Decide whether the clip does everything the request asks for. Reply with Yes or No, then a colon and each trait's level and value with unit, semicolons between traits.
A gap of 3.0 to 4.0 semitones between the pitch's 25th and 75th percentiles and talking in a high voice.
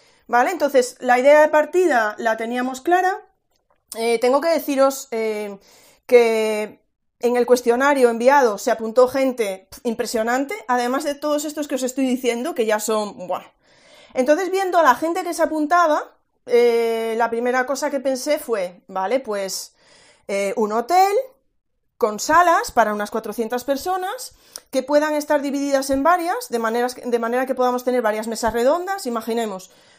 No: average, 4.8 semitones; very high, 250 Hz